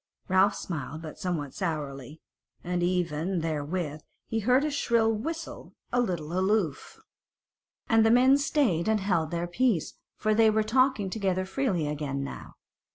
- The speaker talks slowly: No, average, 150 wpm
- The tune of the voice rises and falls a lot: Yes, wide, 5.9 semitones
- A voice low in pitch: No, medium, 185 Hz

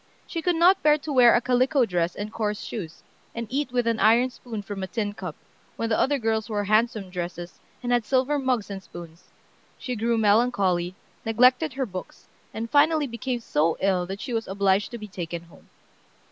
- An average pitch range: Yes, average, 4.6 semitones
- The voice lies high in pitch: Yes, high, 225 Hz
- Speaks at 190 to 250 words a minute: Yes, average, 200 wpm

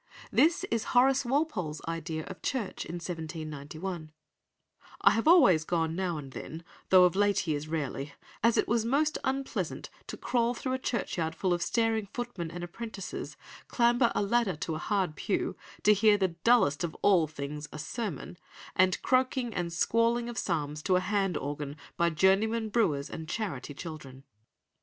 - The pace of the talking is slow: No, average, 170 wpm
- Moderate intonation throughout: No, wide, 6.5 semitones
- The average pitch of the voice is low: No, medium, 185 Hz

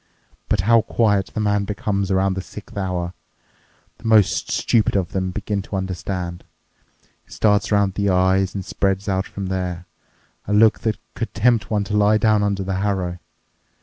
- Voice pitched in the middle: No, low, 100 Hz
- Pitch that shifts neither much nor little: No, narrow, 1.8 semitones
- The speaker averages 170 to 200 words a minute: Yes, average, 175 wpm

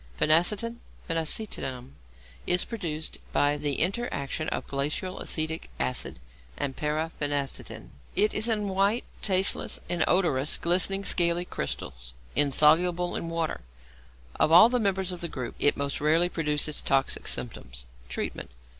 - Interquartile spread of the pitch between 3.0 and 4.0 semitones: No, average, 4.4 semitones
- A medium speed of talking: No, slow, 130 wpm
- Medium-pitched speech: Yes, medium, 165 Hz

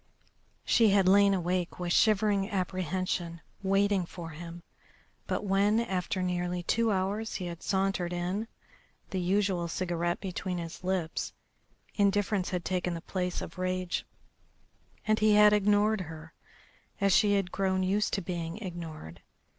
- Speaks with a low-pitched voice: No, medium, 185 Hz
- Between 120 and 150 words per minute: Yes, average, 140 wpm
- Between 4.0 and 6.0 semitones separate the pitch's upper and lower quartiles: No, narrow, 2.5 semitones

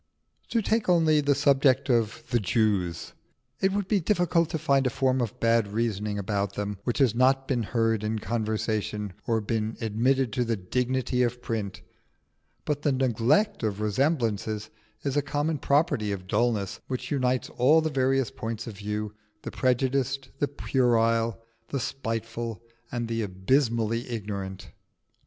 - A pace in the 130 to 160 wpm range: Yes, average, 155 wpm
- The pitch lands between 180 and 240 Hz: No, low, 120 Hz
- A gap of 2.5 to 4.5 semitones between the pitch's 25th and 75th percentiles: Yes, average, 3.9 semitones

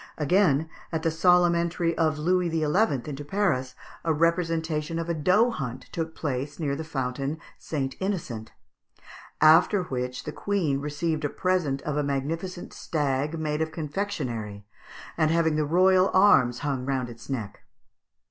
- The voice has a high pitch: No, medium, 155 Hz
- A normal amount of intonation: Yes, average, 3.7 semitones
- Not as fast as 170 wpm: Yes, average, 150 wpm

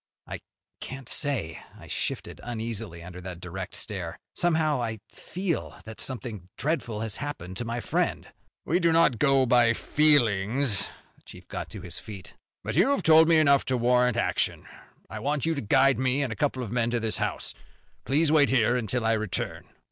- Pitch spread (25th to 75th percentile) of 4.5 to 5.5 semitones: Yes, average, 4.9 semitones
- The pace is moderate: Yes, average, 185 wpm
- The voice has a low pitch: Yes, low, 120 Hz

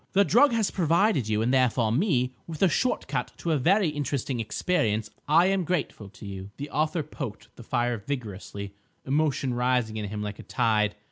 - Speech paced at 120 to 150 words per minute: No, average, 185 wpm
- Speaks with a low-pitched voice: Yes, low, 130 Hz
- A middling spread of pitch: No, wide, 6.9 semitones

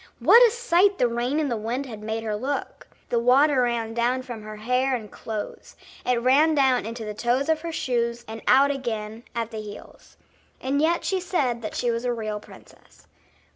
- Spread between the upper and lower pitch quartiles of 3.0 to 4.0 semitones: Yes, average, 3.7 semitones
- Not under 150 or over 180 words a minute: No, fast, 205 wpm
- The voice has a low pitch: No, high, 245 Hz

